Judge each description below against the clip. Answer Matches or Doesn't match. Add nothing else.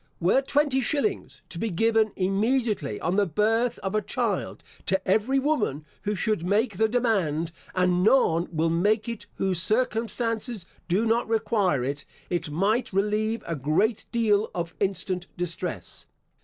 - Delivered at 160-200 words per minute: Doesn't match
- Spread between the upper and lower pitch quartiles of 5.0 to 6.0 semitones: Doesn't match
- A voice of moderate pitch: Doesn't match